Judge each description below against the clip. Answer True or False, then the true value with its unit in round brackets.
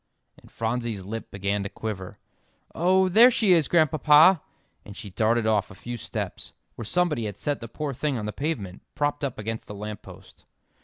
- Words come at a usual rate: True (190 wpm)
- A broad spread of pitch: True (6.4 semitones)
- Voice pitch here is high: False (115 Hz)